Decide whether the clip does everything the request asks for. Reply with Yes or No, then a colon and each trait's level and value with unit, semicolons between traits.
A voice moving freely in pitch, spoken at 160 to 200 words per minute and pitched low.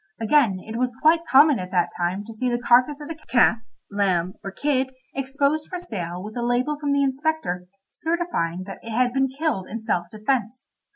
No: wide, 6.0 semitones; average, 195 wpm; high, 245 Hz